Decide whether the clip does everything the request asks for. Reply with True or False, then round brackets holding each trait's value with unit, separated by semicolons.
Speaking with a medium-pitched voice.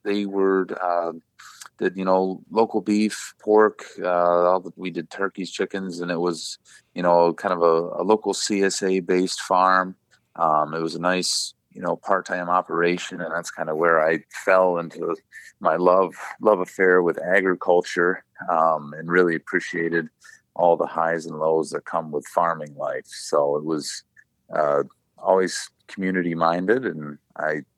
False (90 Hz)